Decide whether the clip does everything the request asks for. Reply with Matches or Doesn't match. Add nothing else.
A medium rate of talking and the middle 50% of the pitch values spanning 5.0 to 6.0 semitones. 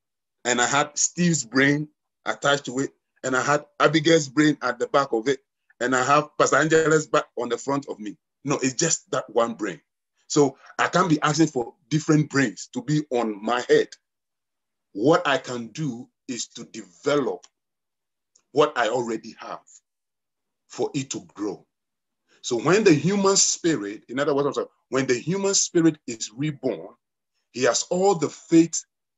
Doesn't match